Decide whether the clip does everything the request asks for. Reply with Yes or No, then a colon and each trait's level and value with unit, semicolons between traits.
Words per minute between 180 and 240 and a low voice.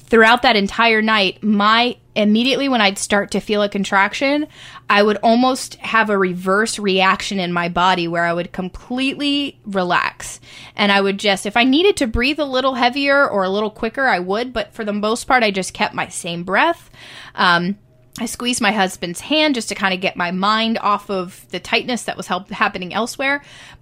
No: average, 200 wpm; high, 210 Hz